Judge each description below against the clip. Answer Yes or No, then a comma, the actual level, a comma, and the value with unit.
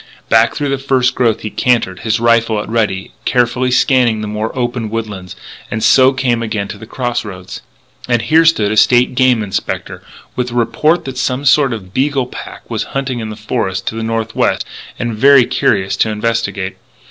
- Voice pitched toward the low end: Yes, low, 115 Hz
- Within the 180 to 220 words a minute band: Yes, average, 195 wpm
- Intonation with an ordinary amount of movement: Yes, average, 3.0 semitones